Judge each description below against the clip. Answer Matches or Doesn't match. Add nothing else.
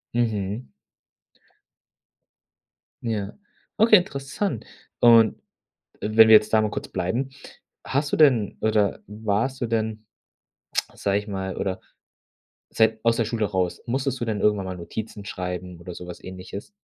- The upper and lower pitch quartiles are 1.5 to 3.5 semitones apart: Matches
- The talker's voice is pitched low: Matches